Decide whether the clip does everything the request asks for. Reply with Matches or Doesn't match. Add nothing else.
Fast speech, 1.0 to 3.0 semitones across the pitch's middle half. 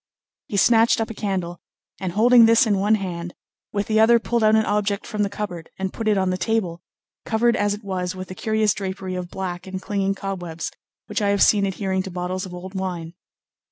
Matches